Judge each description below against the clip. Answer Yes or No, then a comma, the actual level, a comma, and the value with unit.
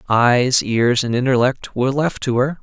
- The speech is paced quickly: No, average, 185 wpm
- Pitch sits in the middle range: No, low, 125 Hz